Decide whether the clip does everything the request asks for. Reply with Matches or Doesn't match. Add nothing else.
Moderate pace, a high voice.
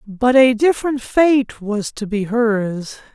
Matches